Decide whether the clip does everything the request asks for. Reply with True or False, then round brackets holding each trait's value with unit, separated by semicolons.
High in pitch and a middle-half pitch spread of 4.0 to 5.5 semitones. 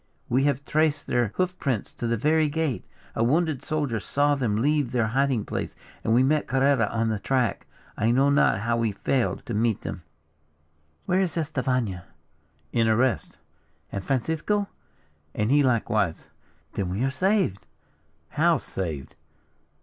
False (130 Hz; 4.7 semitones)